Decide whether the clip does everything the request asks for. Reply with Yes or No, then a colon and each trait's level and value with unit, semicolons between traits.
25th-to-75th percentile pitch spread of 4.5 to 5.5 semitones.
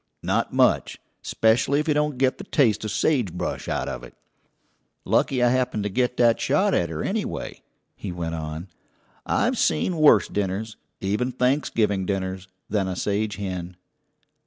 Yes: average, 5.2 semitones